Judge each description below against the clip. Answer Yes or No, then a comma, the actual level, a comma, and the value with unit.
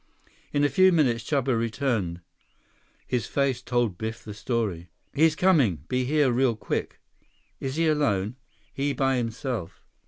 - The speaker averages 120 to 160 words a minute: Yes, average, 145 wpm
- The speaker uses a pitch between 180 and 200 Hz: No, low, 125 Hz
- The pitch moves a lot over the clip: No, average, 4.2 semitones